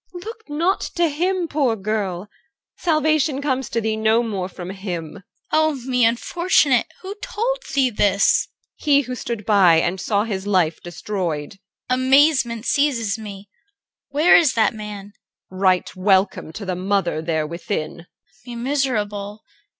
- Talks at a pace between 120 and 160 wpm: Yes, average, 155 wpm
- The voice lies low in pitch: No, high, 220 Hz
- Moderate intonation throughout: No, wide, 6.5 semitones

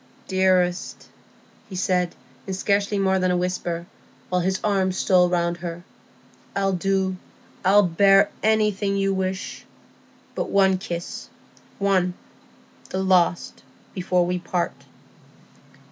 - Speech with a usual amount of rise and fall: No, narrow, 1.5 semitones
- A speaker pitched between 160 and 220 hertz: Yes, medium, 185 Hz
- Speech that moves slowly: Yes, slow, 100 wpm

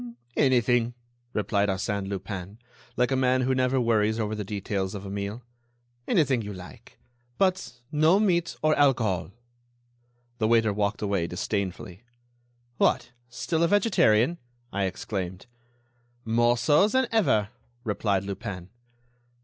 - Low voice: Yes, low, 110 Hz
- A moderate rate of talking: No, slow, 125 wpm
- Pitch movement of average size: Yes, average, 4.6 semitones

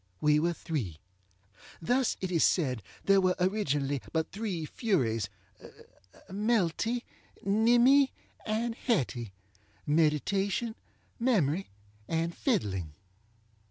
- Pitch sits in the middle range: Yes, medium, 170 Hz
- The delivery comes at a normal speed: No, slow, 85 wpm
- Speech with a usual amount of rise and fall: No, wide, 8.2 semitones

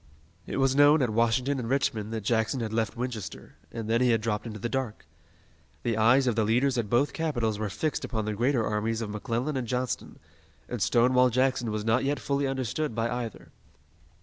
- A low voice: Yes, low, 120 Hz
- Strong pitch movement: No, average, 2.8 semitones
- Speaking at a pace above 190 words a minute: Yes, fast, 205 wpm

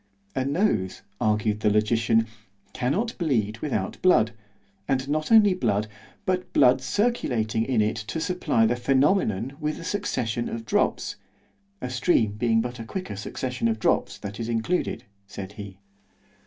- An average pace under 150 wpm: Yes, average, 140 wpm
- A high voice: No, low, 120 Hz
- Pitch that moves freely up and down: Yes, wide, 6.1 semitones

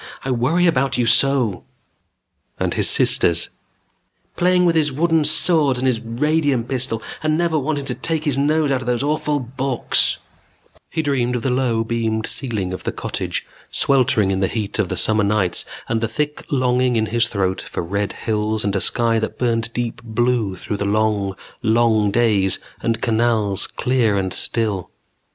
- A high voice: No, low, 120 Hz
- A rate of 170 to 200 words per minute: Yes, average, 180 wpm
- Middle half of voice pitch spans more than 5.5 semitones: No, average, 4.1 semitones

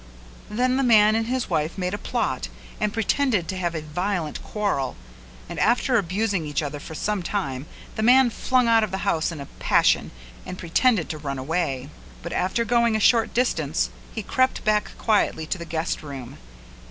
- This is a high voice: Yes, high, 195 Hz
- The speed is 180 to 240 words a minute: Yes, average, 190 wpm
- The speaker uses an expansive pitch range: Yes, wide, 6.1 semitones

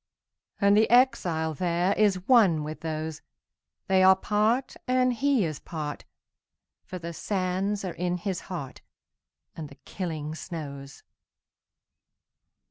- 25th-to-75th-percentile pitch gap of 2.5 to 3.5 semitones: No, average, 4.5 semitones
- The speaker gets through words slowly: Yes, slow, 105 wpm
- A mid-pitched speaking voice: Yes, medium, 180 Hz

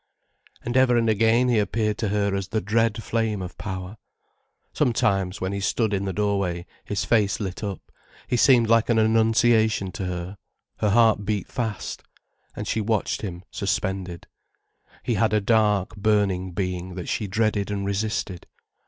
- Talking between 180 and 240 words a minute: No, average, 165 wpm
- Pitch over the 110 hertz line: No, low, 105 Hz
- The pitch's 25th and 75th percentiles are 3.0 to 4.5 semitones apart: No, narrow, 2.6 semitones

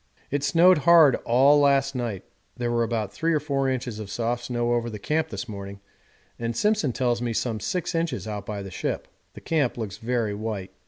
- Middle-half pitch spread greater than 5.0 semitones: No, average, 4.5 semitones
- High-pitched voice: No, low, 120 Hz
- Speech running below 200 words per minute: No, fast, 205 wpm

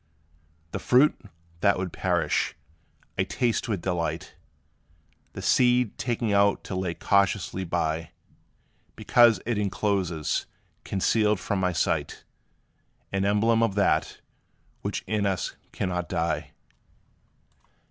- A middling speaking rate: No, slow, 110 wpm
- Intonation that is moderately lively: Yes, average, 3.4 semitones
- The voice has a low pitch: Yes, low, 100 Hz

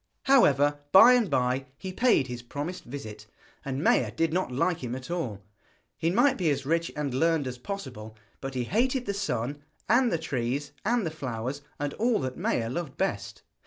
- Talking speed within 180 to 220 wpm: Yes, average, 190 wpm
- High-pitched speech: No, medium, 145 Hz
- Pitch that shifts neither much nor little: No, wide, 6.6 semitones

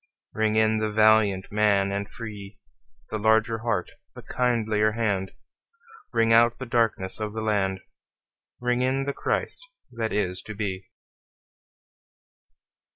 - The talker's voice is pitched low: Yes, low, 110 Hz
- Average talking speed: No, slow, 130 wpm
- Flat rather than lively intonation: Yes, narrow, 2.1 semitones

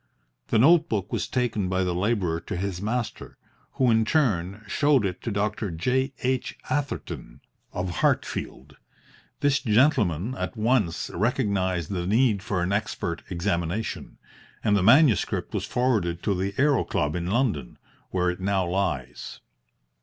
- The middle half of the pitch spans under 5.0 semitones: No, wide, 5.5 semitones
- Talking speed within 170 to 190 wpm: No, average, 145 wpm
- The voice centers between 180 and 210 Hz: No, low, 100 Hz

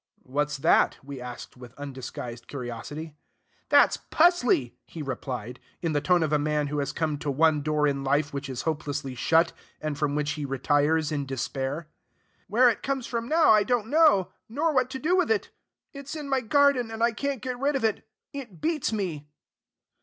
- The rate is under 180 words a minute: No, average, 190 wpm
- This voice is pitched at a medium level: Yes, medium, 155 Hz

